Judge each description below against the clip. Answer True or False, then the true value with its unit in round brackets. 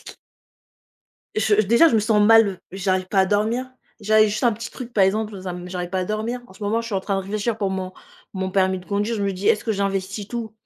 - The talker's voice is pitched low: False (205 Hz)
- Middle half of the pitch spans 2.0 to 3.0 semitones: True (2.5 semitones)